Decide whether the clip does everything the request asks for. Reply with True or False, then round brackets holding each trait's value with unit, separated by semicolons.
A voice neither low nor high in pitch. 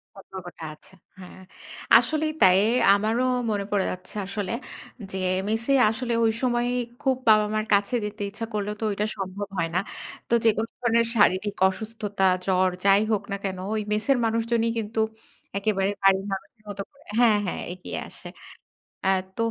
False (210 Hz)